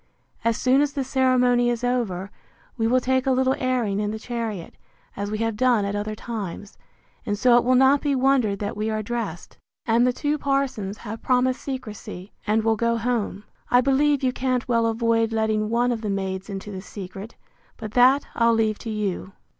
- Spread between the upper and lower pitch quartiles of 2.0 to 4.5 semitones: Yes, average, 3.2 semitones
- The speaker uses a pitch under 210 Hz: No, high, 230 Hz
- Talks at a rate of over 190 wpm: Yes, average, 200 wpm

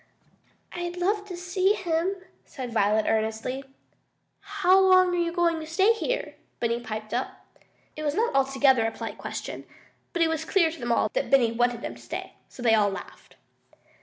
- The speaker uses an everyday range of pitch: No, wide, 7.4 semitones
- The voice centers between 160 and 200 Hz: No, very high, 315 Hz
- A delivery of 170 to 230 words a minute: Yes, average, 180 wpm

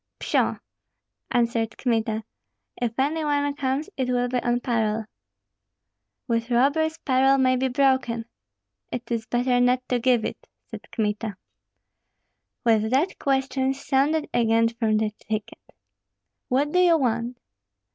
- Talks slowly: Yes, slow, 130 wpm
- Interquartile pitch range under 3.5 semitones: Yes, average, 2.8 semitones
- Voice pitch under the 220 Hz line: No, high, 245 Hz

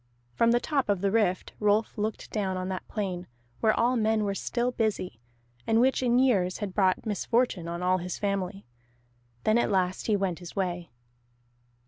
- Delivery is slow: No, average, 180 wpm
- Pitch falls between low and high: No, high, 205 Hz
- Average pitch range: Yes, average, 3.5 semitones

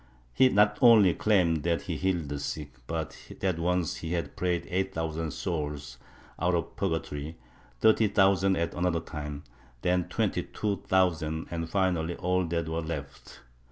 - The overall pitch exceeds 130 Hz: No, very low, 85 Hz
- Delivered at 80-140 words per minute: No, average, 160 wpm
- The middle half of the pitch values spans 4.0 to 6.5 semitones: No, average, 2.8 semitones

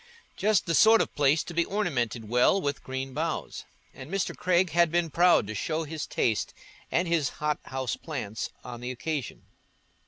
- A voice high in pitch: No, medium, 155 Hz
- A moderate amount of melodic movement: Yes, average, 4.8 semitones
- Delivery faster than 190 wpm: No, average, 175 wpm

